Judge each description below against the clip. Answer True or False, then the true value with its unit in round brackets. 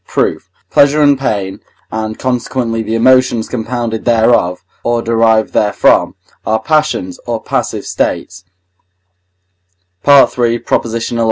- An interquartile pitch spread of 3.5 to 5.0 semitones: False (2.5 semitones)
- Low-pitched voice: True (115 Hz)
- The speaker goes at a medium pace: False (105 wpm)